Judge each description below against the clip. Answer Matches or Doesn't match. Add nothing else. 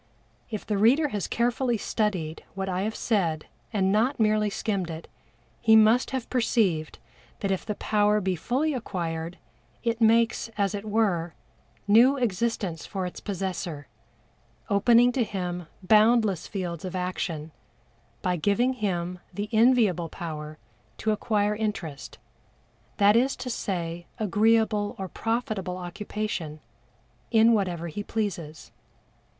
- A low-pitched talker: Doesn't match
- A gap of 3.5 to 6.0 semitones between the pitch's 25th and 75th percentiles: Matches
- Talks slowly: Matches